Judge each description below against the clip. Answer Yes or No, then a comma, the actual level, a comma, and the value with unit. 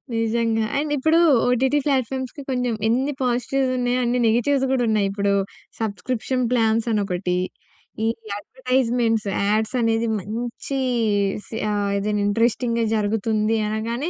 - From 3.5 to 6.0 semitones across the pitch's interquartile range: No, average, 2.8 semitones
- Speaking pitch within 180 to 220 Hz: No, high, 230 Hz